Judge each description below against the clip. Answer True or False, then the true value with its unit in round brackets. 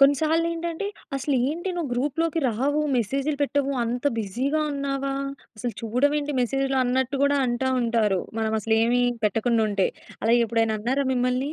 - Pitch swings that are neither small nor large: True (3.6 semitones)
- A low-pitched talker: False (260 Hz)